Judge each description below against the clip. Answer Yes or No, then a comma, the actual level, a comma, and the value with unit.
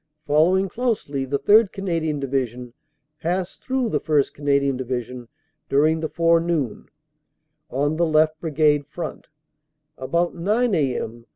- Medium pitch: Yes, medium, 155 Hz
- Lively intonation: No, average, 4.0 semitones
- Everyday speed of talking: No, slow, 120 wpm